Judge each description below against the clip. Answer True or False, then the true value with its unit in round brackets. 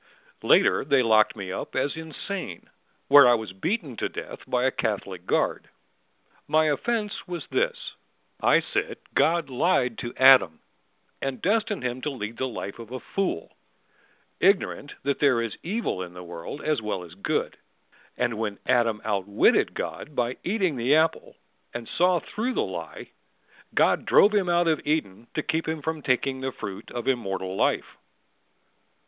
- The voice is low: True (130 Hz)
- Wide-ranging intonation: True (6.7 semitones)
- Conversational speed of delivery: True (165 wpm)